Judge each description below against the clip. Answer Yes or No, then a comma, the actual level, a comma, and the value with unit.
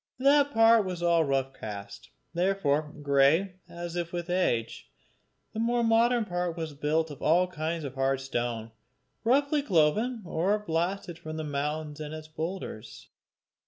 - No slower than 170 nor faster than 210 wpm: No, average, 150 wpm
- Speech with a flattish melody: No, average, 5.0 semitones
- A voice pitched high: No, medium, 165 Hz